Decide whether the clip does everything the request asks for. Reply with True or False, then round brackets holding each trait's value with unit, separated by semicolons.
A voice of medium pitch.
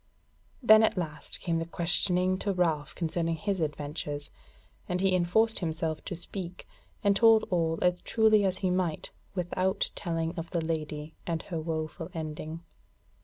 True (170 Hz)